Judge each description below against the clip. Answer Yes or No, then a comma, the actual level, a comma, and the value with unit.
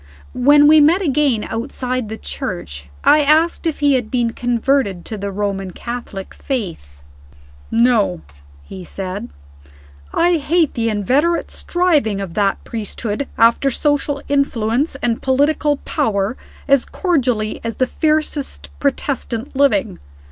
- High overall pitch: Yes, very high, 250 Hz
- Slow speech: Yes, slow, 125 wpm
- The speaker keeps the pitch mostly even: No, wide, 5.5 semitones